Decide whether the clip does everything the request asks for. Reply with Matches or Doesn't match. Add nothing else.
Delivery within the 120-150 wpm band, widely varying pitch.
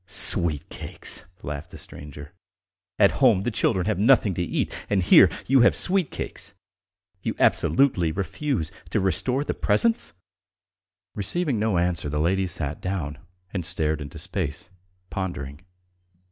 Matches